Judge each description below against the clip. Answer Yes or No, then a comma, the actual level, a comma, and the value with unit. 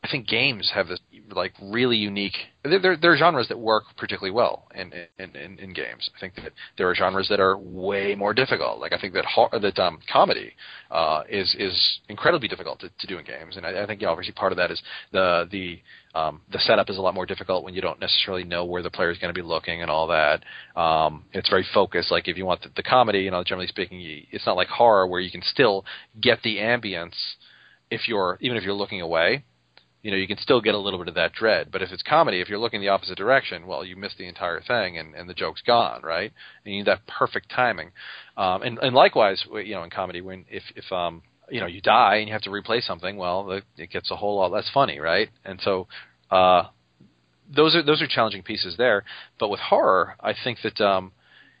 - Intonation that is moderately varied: Yes, average, 3.4 semitones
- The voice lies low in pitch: Yes, low, 100 Hz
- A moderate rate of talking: No, fast, 240 wpm